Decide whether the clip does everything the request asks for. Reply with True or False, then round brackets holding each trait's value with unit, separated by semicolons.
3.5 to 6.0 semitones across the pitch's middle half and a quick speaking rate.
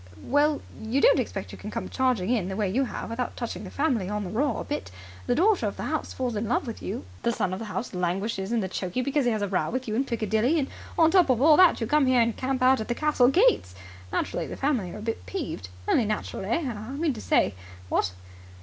True (4.9 semitones; 260 wpm)